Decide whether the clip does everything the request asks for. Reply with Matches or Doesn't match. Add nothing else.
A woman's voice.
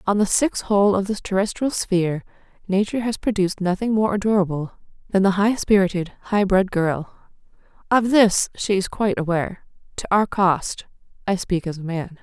Matches